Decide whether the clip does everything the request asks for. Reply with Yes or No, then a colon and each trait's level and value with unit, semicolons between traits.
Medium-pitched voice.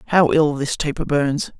Yes: medium, 150 Hz